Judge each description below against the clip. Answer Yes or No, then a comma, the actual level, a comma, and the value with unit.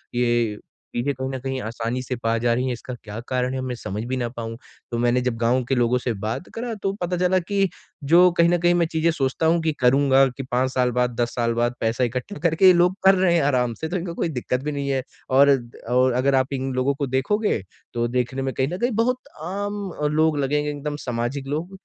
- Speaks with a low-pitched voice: Yes, low, 130 Hz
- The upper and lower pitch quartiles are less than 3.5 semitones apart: No, average, 4.9 semitones